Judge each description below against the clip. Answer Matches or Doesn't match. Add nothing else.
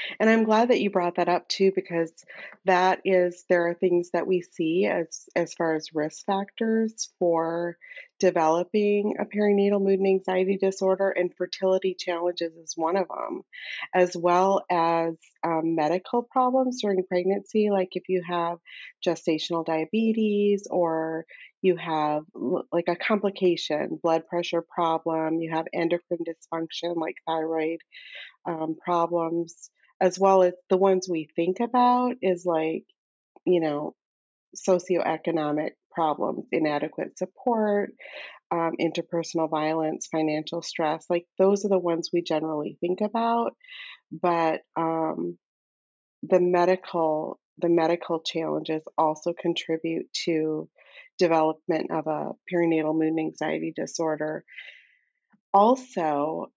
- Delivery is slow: Matches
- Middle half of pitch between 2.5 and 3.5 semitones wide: Matches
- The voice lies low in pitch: Doesn't match